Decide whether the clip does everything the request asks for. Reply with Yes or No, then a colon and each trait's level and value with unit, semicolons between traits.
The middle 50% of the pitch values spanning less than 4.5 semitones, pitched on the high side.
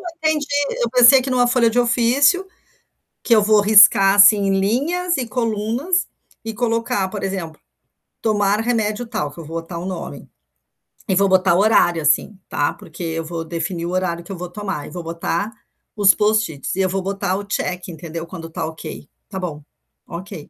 No: average, 5.0 semitones; high, 200 Hz